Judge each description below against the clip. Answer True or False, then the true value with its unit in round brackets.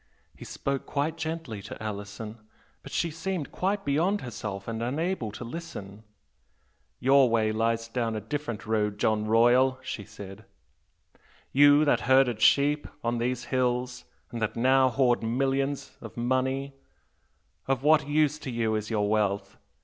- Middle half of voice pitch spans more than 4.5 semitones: False (4.1 semitones)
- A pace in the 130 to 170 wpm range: True (150 wpm)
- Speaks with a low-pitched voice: True (125 Hz)